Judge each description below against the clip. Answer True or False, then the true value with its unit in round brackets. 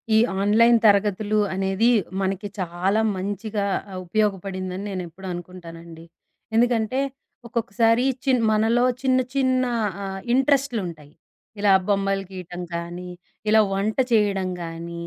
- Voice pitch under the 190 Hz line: False (200 Hz)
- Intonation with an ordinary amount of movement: True (3.7 semitones)